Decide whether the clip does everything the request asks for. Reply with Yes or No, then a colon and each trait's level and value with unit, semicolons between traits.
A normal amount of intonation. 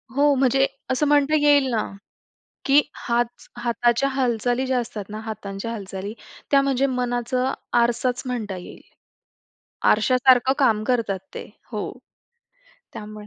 Yes: average, 3.4 semitones